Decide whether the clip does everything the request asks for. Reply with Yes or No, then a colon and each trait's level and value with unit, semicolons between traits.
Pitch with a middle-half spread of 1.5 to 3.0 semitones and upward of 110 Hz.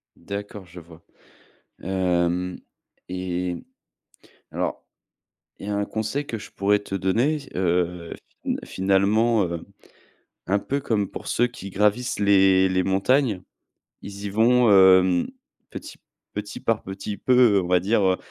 No: average, 2.7 semitones; low, 100 Hz